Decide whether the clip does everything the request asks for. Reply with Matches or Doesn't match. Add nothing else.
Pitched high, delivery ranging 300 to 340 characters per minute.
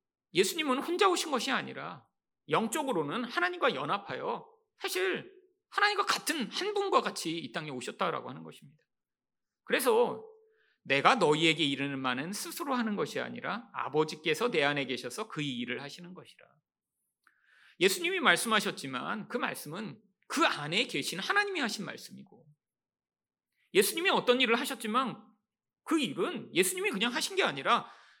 Matches